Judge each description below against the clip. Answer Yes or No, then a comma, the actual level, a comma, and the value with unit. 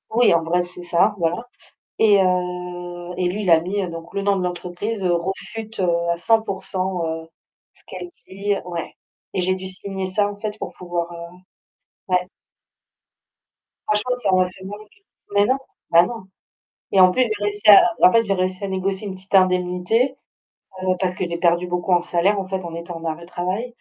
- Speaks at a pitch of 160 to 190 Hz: Yes, medium, 185 Hz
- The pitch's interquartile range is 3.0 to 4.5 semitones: No, narrow, 2.4 semitones